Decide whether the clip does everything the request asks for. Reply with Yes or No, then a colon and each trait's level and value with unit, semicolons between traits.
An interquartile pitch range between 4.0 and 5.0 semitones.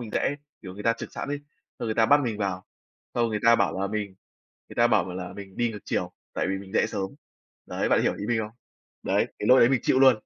No: average, 3.3 semitones